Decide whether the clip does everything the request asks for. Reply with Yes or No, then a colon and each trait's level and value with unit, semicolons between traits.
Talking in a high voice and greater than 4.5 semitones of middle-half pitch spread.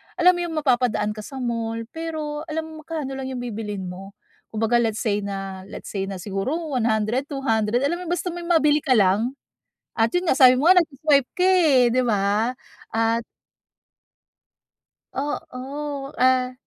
Yes: very high, 255 Hz; wide, 5.5 semitones